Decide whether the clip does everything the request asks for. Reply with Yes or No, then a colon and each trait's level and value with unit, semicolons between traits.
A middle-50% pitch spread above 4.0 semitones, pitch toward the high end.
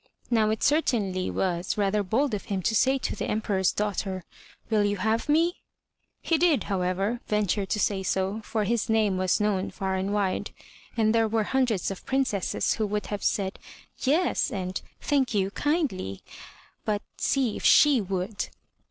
No: average, 3.6 semitones; high, 210 Hz